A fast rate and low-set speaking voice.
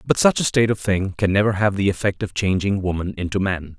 Yes: fast, 255 wpm; low, 100 Hz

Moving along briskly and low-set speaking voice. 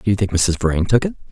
Yes: fast, 320 wpm; low, 100 Hz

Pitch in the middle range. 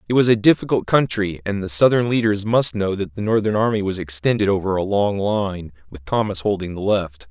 No: low, 100 Hz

